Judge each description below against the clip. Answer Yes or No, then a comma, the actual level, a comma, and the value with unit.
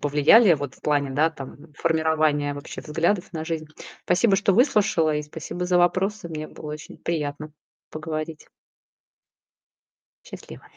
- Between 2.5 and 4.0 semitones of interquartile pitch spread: Yes, average, 2.9 semitones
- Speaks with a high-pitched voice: No, medium, 155 Hz